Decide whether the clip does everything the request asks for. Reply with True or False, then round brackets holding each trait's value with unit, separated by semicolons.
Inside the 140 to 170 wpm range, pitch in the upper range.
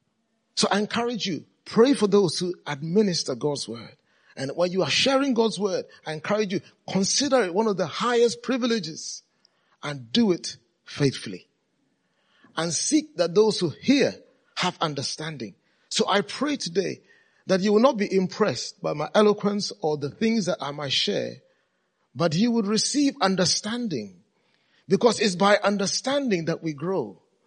True (155 wpm; 200 Hz)